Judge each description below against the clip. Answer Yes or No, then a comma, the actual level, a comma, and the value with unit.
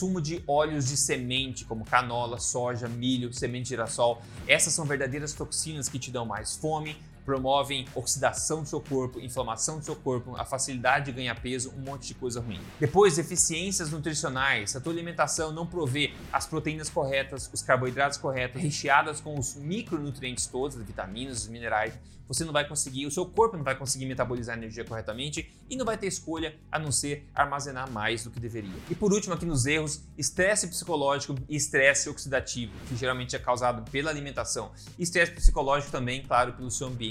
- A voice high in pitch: No, low, 135 Hz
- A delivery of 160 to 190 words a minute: Yes, fast, 185 wpm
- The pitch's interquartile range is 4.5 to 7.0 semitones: No, average, 3.7 semitones